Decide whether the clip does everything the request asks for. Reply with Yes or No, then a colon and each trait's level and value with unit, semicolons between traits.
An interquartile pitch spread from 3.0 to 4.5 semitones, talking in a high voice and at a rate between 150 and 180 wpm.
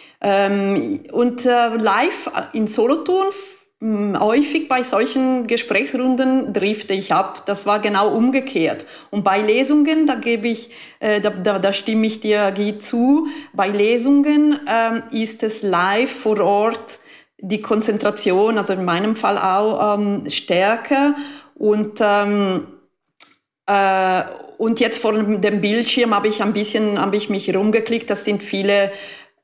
No: average, 3.4 semitones; high, 220 Hz; average, 130 wpm